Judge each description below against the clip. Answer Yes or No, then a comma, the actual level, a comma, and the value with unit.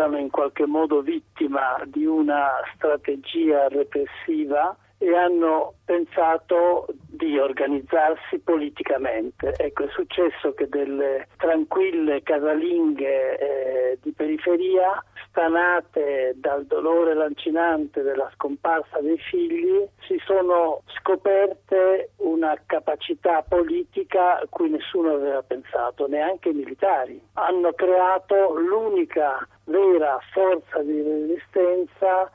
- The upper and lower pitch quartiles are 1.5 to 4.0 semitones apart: No, wide, 5.6 semitones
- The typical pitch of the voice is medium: Yes, medium, 170 Hz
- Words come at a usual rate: No, slow, 100 wpm